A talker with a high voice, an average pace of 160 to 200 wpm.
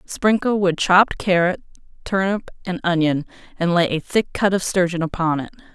No: medium, 180 Hz; average, 165 wpm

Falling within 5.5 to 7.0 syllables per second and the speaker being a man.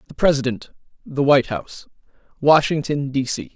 Yes: 5.6 syllables/s; male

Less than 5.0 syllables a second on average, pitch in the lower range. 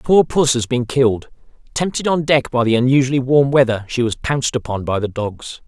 No: 5.5 syllables/s; low, 130 Hz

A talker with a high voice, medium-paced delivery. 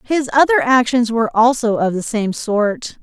Yes: high, 235 Hz; average, 180 wpm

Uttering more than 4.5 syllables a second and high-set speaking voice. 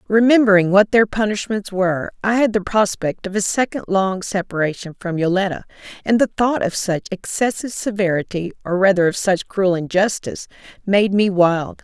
Yes: 5.3 syllables/s; high, 195 Hz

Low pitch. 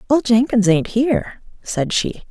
No: high, 230 Hz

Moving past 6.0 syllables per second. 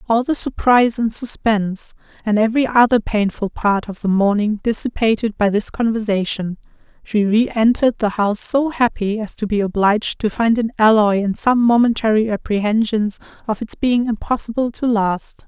No: 5.1 syllables/s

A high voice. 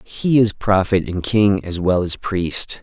No: low, 100 Hz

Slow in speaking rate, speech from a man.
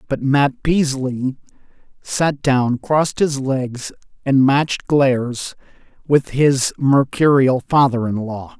Yes: slow, 120 wpm; male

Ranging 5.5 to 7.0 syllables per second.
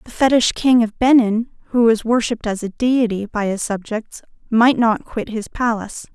No: 5.0 syllables/s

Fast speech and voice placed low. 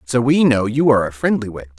Yes: fast, 270 wpm; low, 115 Hz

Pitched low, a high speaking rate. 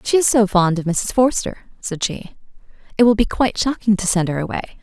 No: high, 210 Hz; fast, 225 wpm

